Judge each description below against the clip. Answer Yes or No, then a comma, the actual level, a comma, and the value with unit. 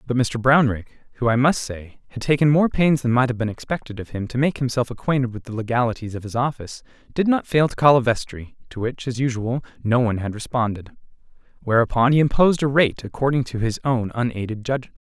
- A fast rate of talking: Yes, fast, 215 wpm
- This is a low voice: Yes, low, 125 Hz